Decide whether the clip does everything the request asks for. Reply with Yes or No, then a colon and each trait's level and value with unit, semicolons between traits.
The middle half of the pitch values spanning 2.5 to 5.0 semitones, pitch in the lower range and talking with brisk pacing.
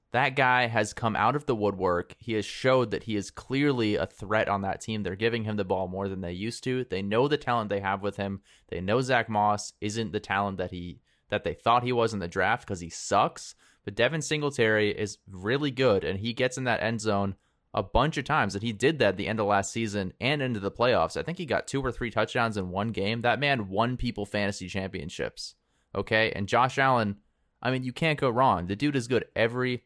Yes: average, 3.9 semitones; low, 110 Hz; fast, 245 wpm